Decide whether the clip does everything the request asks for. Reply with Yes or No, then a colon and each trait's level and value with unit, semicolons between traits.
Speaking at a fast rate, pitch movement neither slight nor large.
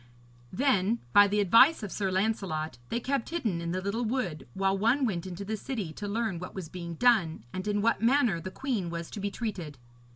Yes: fast, 215 wpm; average, 4.4 semitones